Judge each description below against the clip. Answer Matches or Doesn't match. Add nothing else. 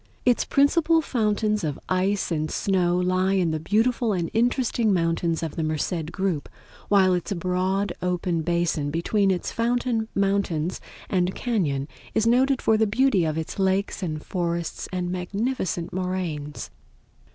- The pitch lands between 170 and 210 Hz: Matches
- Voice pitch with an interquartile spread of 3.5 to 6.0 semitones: Matches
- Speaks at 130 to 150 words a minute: Matches